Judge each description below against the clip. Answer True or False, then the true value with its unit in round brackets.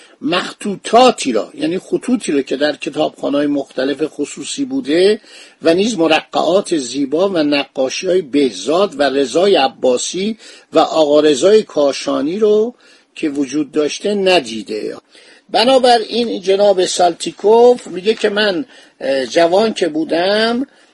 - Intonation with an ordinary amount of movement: False (7.7 semitones)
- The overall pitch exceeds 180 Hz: True (190 Hz)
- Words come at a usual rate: True (115 wpm)